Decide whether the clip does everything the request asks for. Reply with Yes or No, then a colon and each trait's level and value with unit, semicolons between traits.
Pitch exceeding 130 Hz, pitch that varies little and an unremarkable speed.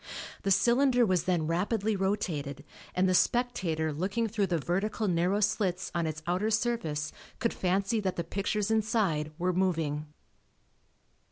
No: medium, 185 Hz; average, 4.2 semitones; average, 145 wpm